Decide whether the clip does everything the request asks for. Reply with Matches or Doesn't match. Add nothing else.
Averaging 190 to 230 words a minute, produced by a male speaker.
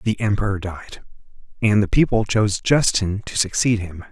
Doesn't match